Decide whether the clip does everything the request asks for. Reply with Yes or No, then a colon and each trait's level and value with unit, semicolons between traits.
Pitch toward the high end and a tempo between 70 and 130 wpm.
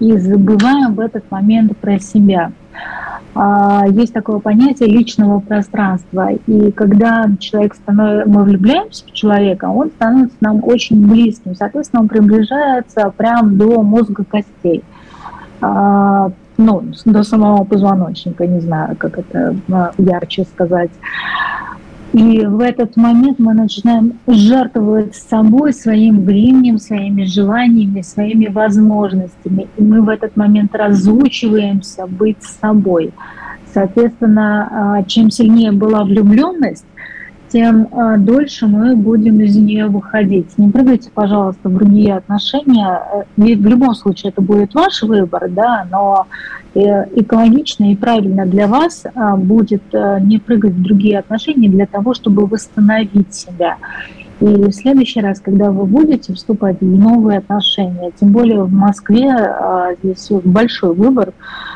Yes: high, 210 Hz; average, 120 wpm